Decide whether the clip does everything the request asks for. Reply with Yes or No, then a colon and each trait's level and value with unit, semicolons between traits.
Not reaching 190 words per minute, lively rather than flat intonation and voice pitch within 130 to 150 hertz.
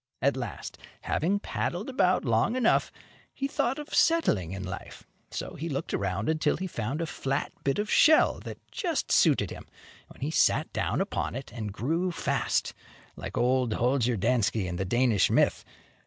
Yes: average, 170 wpm; wide, 8.5 semitones; low, 135 Hz